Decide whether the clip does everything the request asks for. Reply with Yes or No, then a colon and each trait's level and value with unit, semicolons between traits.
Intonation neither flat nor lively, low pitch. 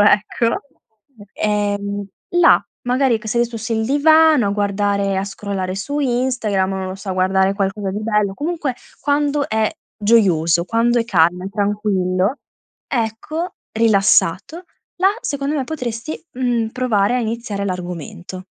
No: average, 4.2 semitones; high, 215 Hz